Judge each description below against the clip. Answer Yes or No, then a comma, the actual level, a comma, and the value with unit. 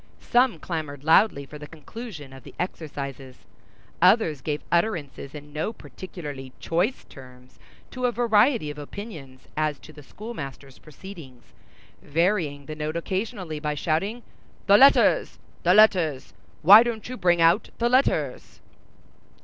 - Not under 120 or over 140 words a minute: Yes, slow, 135 wpm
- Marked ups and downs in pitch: Yes, wide, 6.5 semitones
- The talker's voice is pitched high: No, medium, 160 Hz